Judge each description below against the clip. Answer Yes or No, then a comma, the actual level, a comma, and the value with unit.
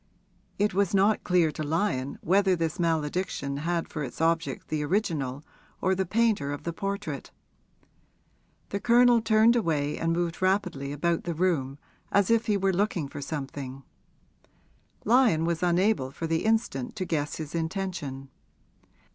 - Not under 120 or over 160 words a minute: Yes, average, 150 wpm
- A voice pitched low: No, medium, 170 Hz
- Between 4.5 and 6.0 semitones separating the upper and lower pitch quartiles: Yes, average, 5.1 semitones